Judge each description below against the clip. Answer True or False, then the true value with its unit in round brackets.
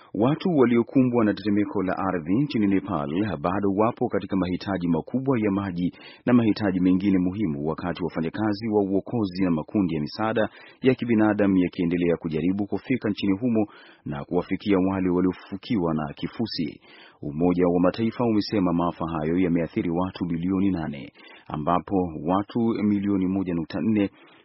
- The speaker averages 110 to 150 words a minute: True (135 wpm)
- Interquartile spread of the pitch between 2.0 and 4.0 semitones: True (3.2 semitones)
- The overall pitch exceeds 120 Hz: False (95 Hz)